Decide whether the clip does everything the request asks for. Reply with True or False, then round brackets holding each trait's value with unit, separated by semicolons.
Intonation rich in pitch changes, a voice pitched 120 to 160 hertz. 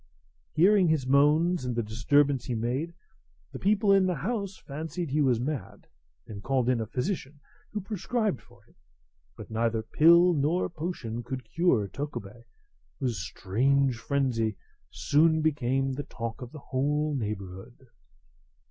True (5.7 semitones; 140 Hz)